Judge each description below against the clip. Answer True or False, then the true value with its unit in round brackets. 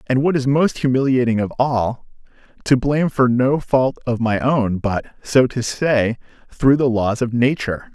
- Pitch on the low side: True (125 Hz)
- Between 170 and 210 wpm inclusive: True (180 wpm)